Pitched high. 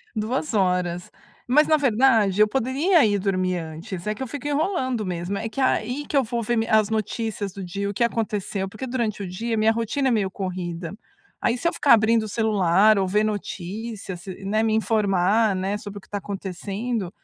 Yes: high, 215 Hz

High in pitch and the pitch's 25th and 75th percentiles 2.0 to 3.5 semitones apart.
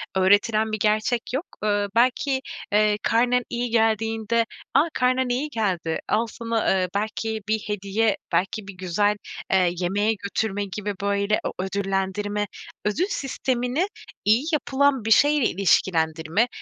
Yes: high, 215 Hz; average, 3.0 semitones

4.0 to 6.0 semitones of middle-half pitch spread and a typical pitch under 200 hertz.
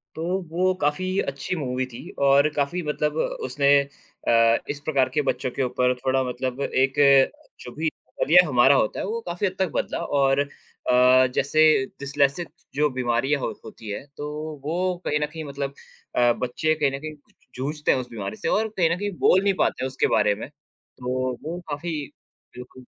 No: average, 3.6 semitones; medium, 140 Hz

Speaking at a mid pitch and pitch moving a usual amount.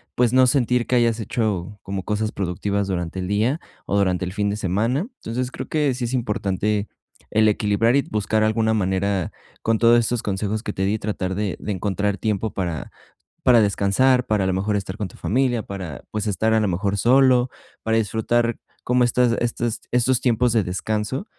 No: low, 110 Hz; average, 3.2 semitones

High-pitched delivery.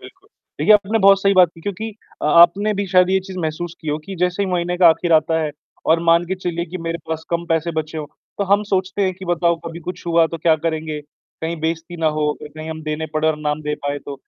No: medium, 170 Hz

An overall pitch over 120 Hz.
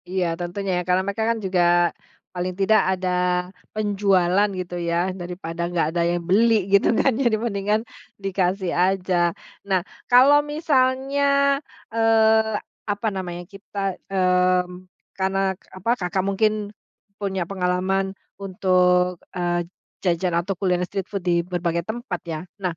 Yes: high, 190 Hz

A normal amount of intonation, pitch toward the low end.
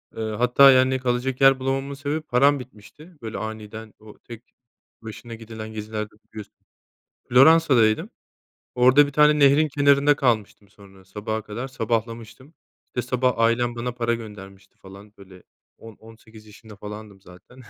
Yes: average, 3.6 semitones; low, 115 Hz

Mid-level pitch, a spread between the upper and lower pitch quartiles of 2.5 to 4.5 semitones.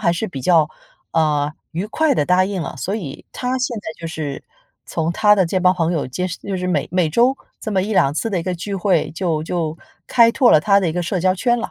Yes: medium, 180 Hz; average, 4.1 semitones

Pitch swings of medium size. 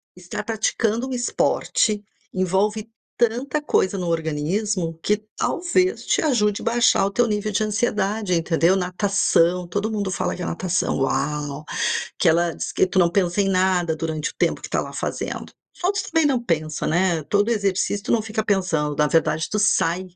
Yes: average, 4.2 semitones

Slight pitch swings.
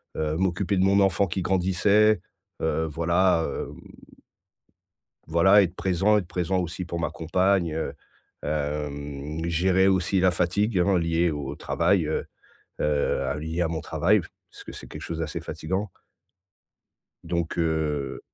No: average, 3.0 semitones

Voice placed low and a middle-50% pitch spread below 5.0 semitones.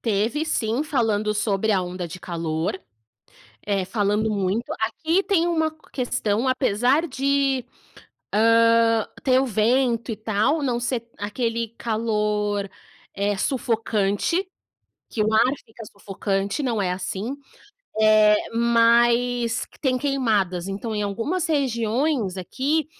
No: high, 225 Hz; average, 3.8 semitones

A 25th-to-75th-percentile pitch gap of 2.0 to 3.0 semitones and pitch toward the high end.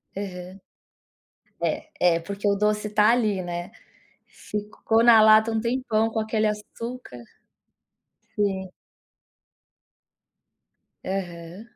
Yes: narrow, 2.6 semitones; high, 210 Hz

